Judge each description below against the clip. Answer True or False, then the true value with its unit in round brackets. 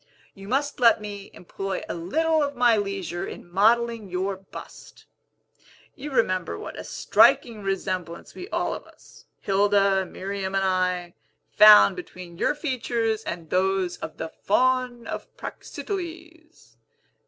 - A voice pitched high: True (200 Hz)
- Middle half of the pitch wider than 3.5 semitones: True (4.7 semitones)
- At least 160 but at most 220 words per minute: False (135 wpm)